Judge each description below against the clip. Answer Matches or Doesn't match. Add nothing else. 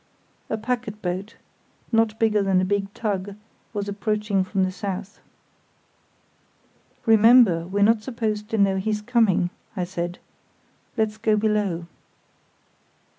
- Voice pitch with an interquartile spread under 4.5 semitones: Matches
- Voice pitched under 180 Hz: Doesn't match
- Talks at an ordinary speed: Doesn't match